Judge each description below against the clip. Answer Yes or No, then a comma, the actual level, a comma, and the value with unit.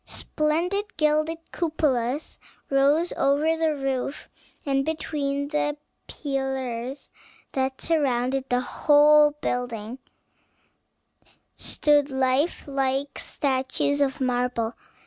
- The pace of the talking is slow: Yes, slow, 90 wpm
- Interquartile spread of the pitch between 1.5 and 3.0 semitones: Yes, narrow, 2.4 semitones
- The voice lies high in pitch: Yes, very high, 275 Hz